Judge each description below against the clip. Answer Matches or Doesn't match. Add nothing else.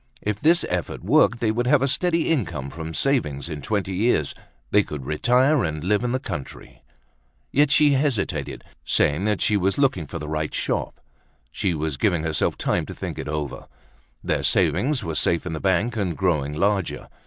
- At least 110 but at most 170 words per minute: Doesn't match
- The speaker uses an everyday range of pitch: Doesn't match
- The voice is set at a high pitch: Doesn't match